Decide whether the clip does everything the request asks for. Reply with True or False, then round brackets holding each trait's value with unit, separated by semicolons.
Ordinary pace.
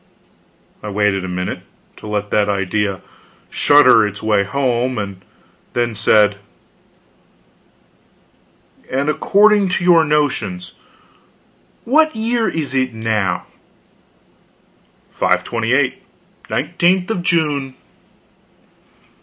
False (90 wpm)